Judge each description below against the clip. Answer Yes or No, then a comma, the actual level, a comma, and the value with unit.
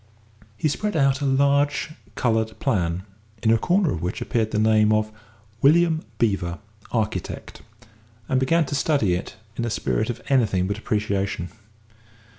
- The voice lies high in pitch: No, low, 110 Hz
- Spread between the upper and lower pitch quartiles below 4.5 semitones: No, wide, 5.4 semitones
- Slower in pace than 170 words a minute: Yes, average, 150 wpm